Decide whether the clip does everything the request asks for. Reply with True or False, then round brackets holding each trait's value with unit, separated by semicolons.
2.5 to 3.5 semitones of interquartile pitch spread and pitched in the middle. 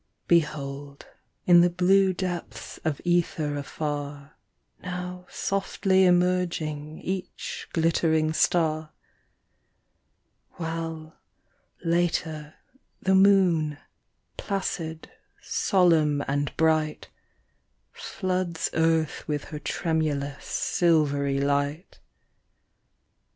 True (3.0 semitones; 160 Hz)